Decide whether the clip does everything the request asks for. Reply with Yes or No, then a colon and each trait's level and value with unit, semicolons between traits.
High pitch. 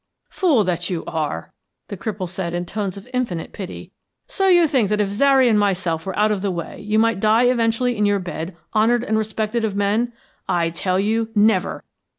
Yes: high, 210 Hz